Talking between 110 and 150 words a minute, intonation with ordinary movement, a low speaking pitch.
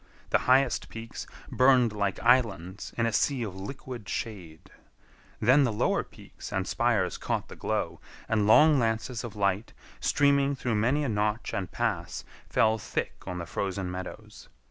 No: average, 160 wpm; average, 4.4 semitones; low, 110 Hz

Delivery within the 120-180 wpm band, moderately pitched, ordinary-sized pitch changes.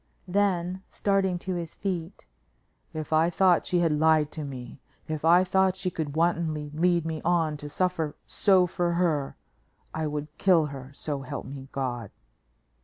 Yes: average, 165 wpm; medium, 165 Hz; average, 3.2 semitones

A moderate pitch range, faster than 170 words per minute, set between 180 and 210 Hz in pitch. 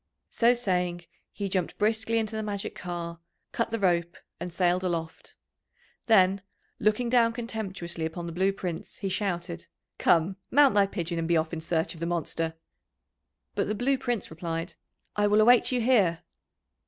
No: average, 4.3 semitones; average, 165 wpm; medium, 185 Hz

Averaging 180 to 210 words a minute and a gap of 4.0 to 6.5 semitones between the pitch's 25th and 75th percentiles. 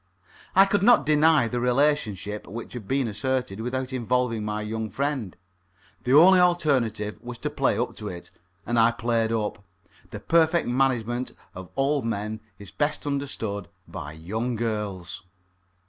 No: average, 150 wpm; average, 4.7 semitones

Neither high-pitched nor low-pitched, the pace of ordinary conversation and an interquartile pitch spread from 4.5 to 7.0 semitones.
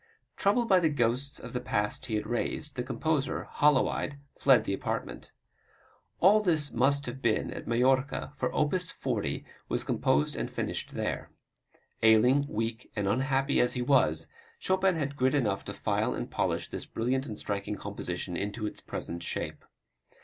No: low, 130 Hz; average, 165 wpm; average, 4.8 semitones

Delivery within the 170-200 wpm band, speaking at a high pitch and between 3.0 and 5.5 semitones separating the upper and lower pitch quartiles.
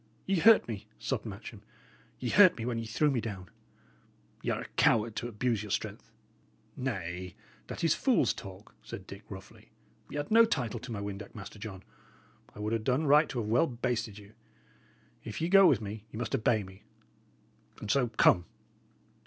No: average, 185 wpm; low, 115 Hz; average, 4.2 semitones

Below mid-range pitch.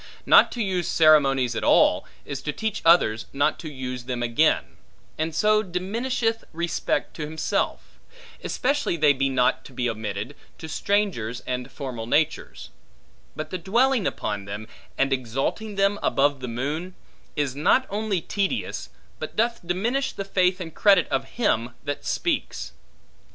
No: medium, 155 Hz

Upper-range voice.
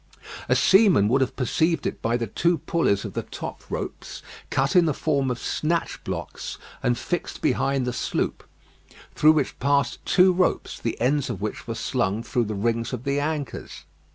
No: low, 135 Hz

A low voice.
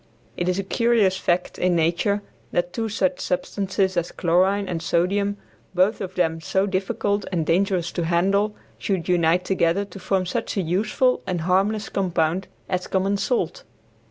No: medium, 185 Hz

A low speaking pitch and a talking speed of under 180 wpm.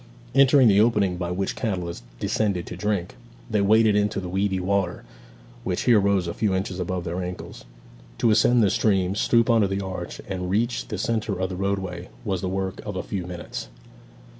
No: very low, 95 Hz; average, 190 wpm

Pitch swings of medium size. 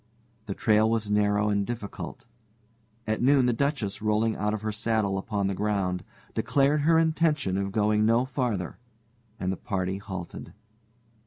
Yes: average, 3.3 semitones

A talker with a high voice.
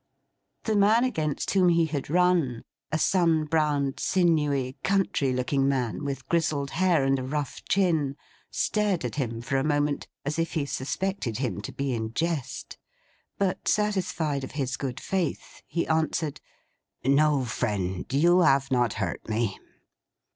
No: medium, 145 Hz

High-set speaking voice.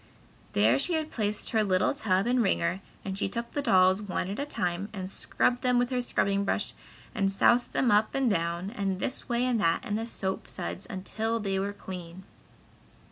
Yes: high, 205 Hz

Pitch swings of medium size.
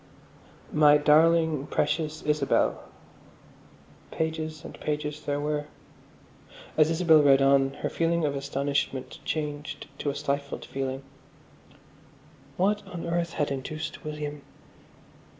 No: narrow, 2.0 semitones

